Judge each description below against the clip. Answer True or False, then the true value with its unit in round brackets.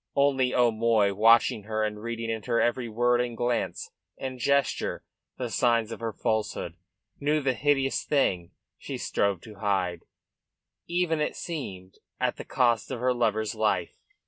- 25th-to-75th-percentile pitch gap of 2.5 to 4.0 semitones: True (3.2 semitones)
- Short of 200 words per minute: True (155 wpm)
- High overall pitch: False (115 Hz)